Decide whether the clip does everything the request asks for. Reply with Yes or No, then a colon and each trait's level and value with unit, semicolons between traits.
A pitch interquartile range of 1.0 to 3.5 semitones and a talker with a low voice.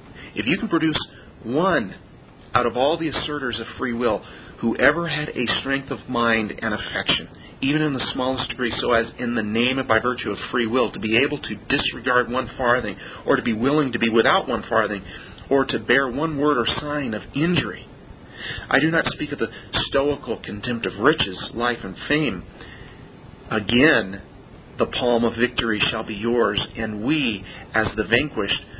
Yes: average, 3.0 semitones; low, 125 Hz